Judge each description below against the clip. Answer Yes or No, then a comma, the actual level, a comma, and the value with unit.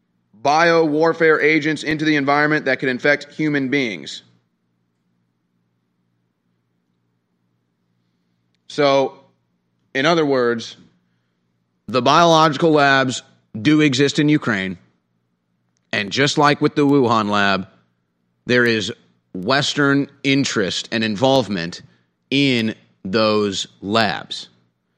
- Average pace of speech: No, slow, 90 wpm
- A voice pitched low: Yes, low, 105 Hz